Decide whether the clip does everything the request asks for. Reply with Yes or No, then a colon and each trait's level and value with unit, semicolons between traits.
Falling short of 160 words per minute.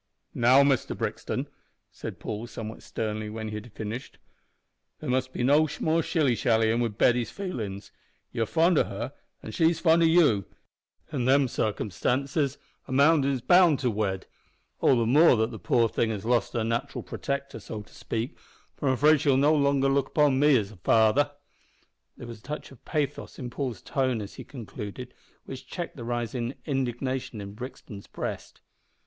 No: average, 180 wpm